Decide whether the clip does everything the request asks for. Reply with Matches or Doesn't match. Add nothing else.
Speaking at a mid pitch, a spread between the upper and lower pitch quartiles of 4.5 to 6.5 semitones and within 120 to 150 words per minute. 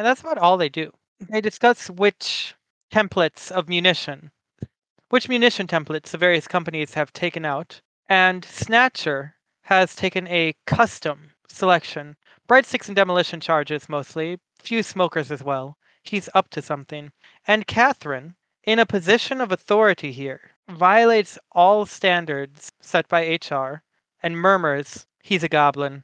Matches